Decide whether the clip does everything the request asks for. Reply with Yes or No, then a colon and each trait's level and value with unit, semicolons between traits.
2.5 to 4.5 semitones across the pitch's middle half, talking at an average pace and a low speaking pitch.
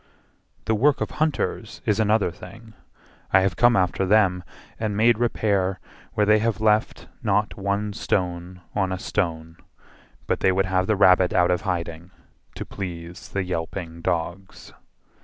Yes: average, 3.0 semitones; average, 155 wpm; very low, 95 Hz